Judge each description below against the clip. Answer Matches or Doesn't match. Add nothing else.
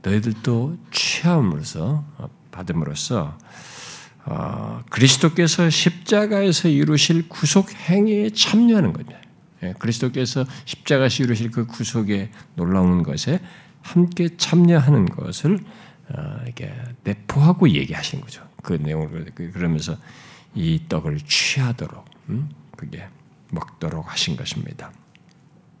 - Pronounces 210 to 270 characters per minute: Matches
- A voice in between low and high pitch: Matches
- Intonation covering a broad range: Matches